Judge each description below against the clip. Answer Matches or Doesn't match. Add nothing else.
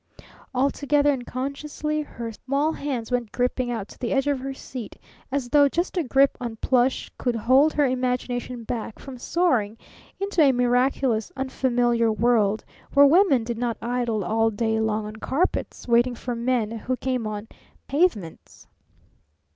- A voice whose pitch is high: Matches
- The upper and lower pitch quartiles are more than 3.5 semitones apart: Doesn't match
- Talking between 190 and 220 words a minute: Doesn't match